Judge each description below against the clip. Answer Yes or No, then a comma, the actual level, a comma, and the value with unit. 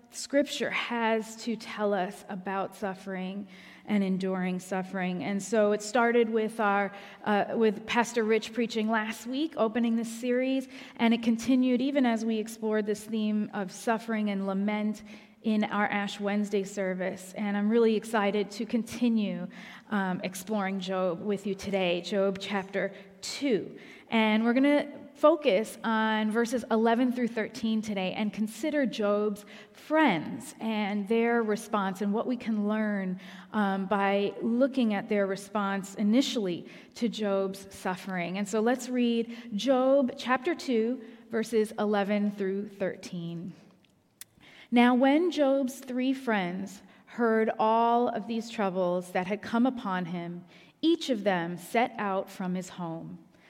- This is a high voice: Yes, high, 215 Hz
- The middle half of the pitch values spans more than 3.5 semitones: No, average, 3.0 semitones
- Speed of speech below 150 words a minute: Yes, average, 140 wpm